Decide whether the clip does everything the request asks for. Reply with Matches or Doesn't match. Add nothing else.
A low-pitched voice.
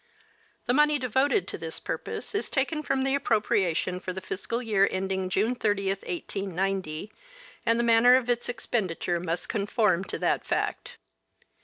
Doesn't match